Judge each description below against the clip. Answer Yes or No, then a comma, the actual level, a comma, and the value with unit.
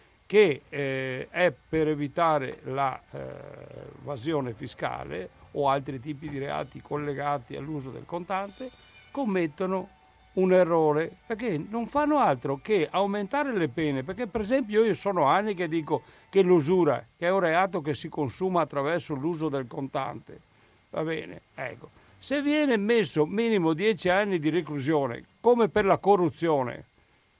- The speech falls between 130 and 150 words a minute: Yes, average, 140 wpm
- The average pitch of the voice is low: No, medium, 170 Hz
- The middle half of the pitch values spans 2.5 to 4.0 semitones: No, wide, 5.5 semitones